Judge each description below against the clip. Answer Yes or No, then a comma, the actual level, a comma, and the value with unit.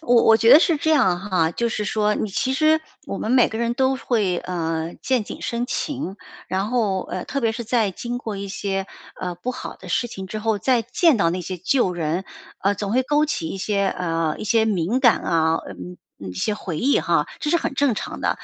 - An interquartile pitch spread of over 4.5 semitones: Yes, average, 5.2 semitones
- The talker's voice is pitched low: No, high, 215 Hz